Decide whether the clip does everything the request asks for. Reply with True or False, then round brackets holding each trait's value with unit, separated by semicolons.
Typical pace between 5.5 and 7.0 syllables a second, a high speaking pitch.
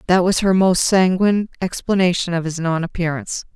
False (5.7 syllables/s; 180 Hz)